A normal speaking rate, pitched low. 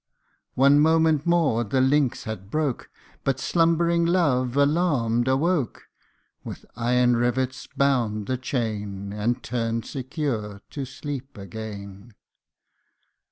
No: slow, 110 wpm; low, 130 Hz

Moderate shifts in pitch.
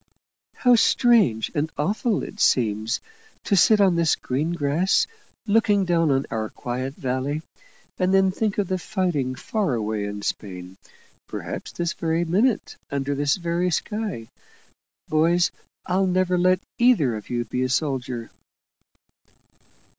No: wide, 6.7 semitones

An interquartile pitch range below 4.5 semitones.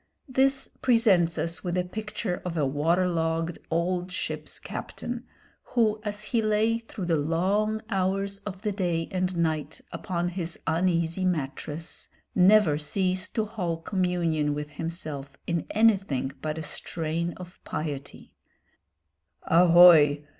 Yes: average, 3.6 semitones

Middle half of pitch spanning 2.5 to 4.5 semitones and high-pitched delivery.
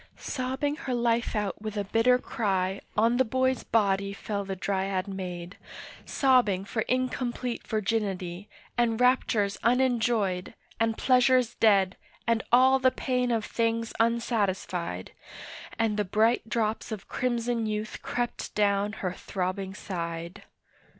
Yes: average, 3.7 semitones; high, 220 Hz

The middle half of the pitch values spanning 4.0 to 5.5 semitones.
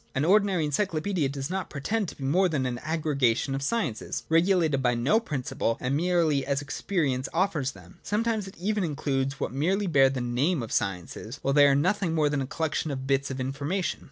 Yes: average, 5.1 semitones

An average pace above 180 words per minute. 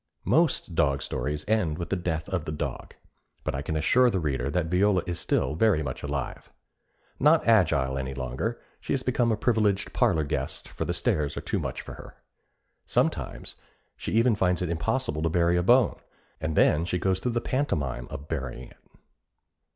Yes: average, 190 wpm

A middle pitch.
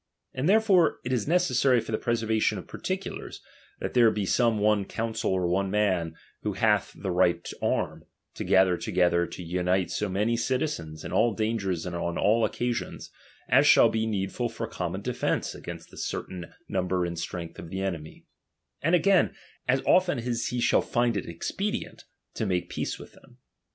No: low, 105 Hz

